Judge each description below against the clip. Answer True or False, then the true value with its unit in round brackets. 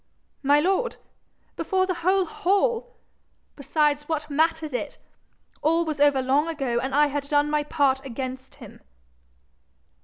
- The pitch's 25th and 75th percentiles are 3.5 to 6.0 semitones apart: False (3.1 semitones)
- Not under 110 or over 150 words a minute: True (140 wpm)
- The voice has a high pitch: True (295 Hz)